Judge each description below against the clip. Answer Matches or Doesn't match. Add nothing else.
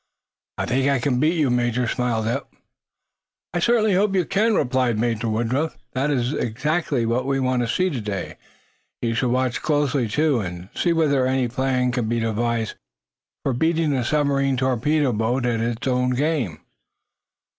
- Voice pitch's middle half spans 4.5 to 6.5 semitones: Doesn't match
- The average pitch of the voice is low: Matches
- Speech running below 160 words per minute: Doesn't match